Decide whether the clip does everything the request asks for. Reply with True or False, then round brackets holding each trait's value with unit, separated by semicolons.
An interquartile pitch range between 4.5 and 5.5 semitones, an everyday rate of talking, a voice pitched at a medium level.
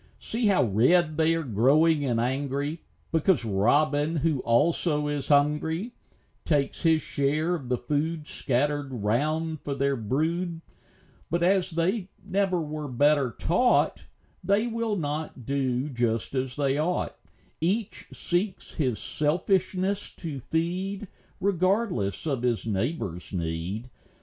False (4.9 semitones; 125 wpm; 150 Hz)